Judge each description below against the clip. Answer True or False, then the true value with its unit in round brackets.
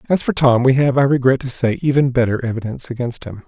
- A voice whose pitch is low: True (130 Hz)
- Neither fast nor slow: False (240 wpm)